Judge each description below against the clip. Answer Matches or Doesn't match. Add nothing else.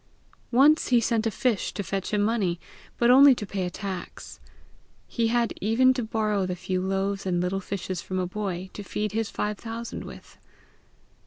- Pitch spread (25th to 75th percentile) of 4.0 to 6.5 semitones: Doesn't match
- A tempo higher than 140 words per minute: Matches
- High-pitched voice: Matches